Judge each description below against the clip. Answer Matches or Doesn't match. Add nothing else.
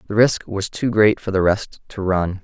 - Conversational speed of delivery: Doesn't match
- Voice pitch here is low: Matches